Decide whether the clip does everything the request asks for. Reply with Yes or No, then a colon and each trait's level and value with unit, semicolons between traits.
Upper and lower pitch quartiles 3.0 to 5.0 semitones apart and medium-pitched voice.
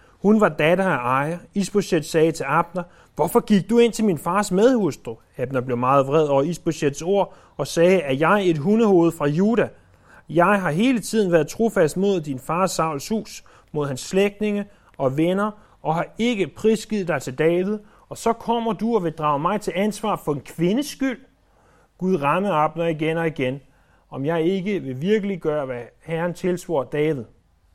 No: wide, 5.5 semitones; medium, 175 Hz